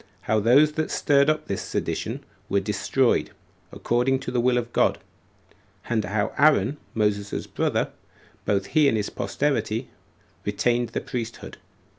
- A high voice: No, low, 120 Hz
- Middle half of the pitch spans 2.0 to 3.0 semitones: No, average, 4.4 semitones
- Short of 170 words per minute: Yes, average, 140 wpm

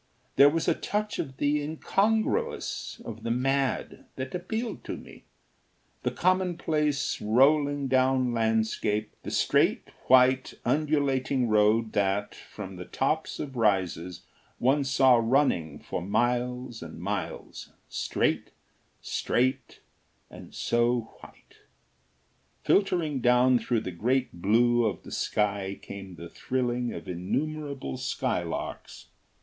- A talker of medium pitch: No, low, 125 Hz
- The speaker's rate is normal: No, slow, 115 wpm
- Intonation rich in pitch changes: No, average, 4.6 semitones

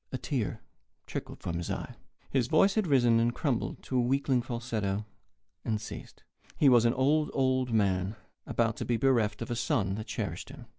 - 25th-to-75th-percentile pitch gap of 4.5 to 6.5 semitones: No, average, 3.4 semitones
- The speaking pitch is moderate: No, low, 120 Hz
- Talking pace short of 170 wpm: No, average, 190 wpm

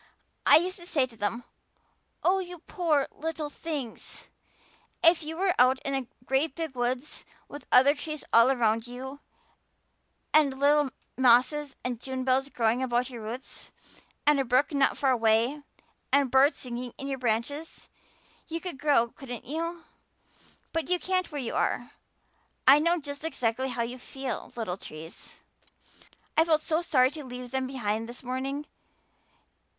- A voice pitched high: Yes, very high, 270 Hz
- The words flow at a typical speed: Yes, average, 155 wpm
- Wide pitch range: No, average, 3.7 semitones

